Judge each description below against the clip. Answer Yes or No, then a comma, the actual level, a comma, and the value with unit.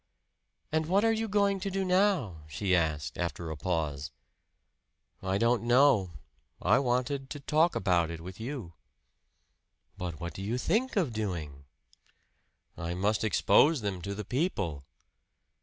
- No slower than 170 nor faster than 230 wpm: No, average, 145 wpm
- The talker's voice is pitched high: No, low, 105 Hz